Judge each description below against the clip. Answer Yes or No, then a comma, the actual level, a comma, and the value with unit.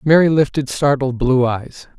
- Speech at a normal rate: Yes, average, 150 wpm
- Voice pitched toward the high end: No, low, 135 Hz